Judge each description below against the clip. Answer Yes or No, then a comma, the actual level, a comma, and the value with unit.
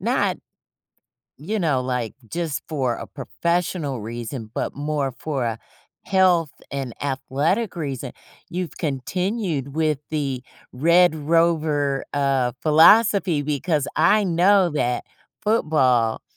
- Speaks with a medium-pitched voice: Yes, medium, 150 Hz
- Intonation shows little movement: No, average, 4.4 semitones